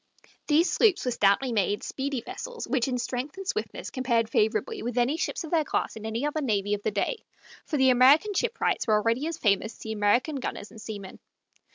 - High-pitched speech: Yes, very high, 250 Hz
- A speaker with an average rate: No, fast, 210 wpm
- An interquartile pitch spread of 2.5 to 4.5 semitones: No, wide, 5.6 semitones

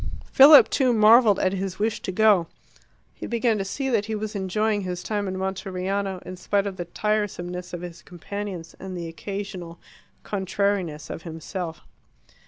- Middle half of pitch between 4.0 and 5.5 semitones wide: No, average, 2.8 semitones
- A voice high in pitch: Yes, high, 195 Hz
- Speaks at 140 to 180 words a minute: Yes, average, 165 wpm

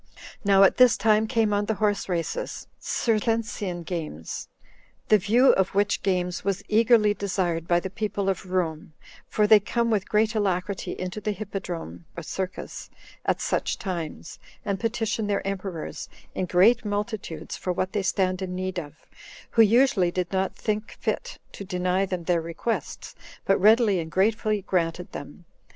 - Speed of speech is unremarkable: Yes, average, 160 wpm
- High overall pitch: Yes, high, 195 Hz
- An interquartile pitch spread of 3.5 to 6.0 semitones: No, average, 3.0 semitones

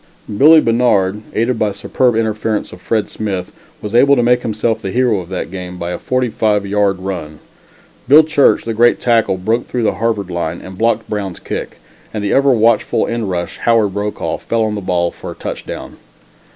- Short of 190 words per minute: No, average, 195 wpm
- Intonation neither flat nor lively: Yes, average, 3.5 semitones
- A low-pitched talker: Yes, low, 110 Hz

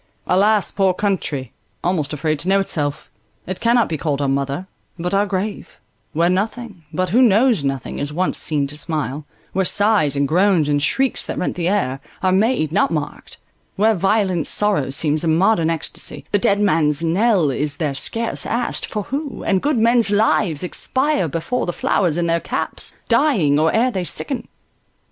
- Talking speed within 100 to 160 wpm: No, average, 180 wpm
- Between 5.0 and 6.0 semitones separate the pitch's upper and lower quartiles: Yes, wide, 5.5 semitones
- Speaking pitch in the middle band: Yes, medium, 180 Hz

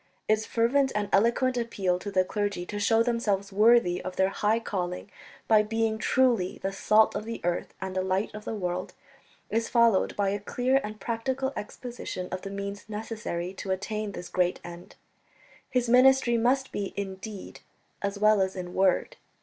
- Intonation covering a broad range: No, average, 3.4 semitones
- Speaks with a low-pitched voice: No, high, 210 Hz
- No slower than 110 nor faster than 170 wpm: No, average, 180 wpm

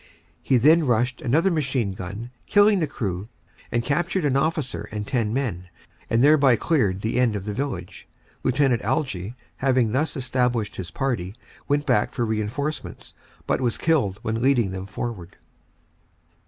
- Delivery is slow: No, average, 155 wpm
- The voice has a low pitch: Yes, low, 120 Hz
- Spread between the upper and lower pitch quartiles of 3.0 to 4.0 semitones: No, average, 4.9 semitones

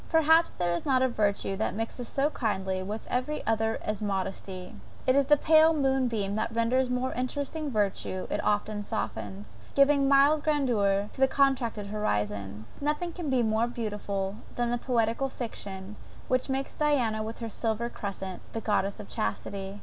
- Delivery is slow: No, average, 170 wpm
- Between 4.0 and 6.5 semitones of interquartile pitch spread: Yes, average, 5.2 semitones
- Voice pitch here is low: No, high, 225 Hz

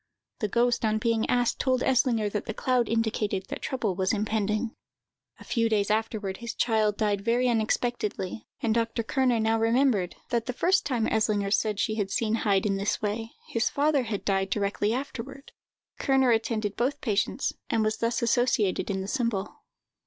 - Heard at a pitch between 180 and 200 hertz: No, high, 225 Hz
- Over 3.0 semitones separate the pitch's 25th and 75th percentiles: No, narrow, 2.6 semitones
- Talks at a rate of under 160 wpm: No, average, 175 wpm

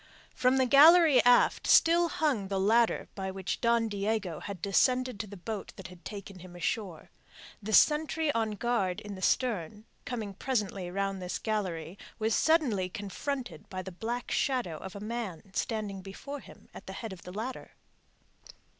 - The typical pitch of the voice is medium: No, high, 210 Hz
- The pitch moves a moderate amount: Yes, average, 4.4 semitones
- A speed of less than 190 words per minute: Yes, average, 170 wpm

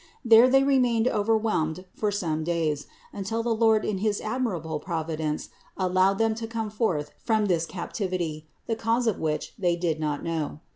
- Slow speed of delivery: No, average, 165 wpm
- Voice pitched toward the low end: No, high, 195 Hz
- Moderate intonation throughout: No, wide, 5.7 semitones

